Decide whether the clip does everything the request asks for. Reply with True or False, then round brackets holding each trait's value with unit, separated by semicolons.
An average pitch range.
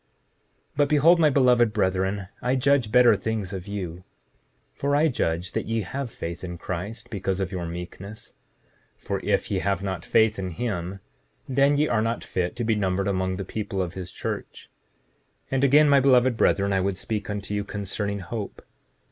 True (4.8 semitones)